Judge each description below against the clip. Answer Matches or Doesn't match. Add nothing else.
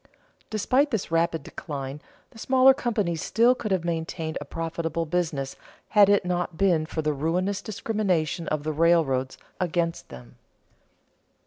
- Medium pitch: Matches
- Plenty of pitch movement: Doesn't match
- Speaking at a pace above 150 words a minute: Doesn't match